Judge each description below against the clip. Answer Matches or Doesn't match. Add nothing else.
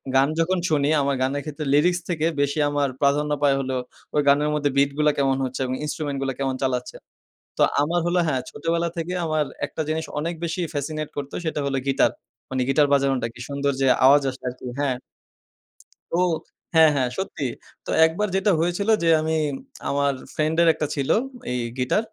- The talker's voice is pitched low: Doesn't match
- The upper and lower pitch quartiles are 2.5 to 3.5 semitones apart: Matches